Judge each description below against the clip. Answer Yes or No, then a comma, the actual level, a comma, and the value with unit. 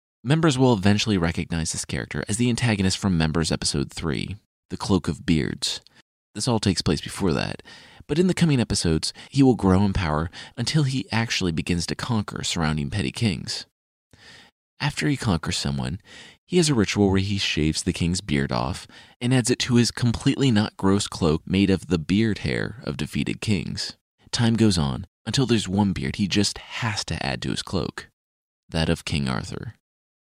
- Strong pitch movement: Yes, wide, 5.9 semitones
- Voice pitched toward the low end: Yes, low, 100 Hz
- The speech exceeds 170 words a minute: Yes, average, 185 wpm